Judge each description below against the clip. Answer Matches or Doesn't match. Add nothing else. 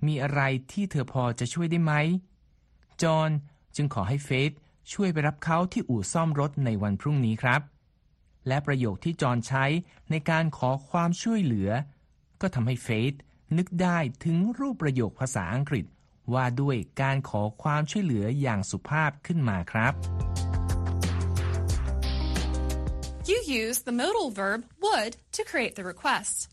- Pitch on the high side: Doesn't match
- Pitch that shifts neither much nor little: Doesn't match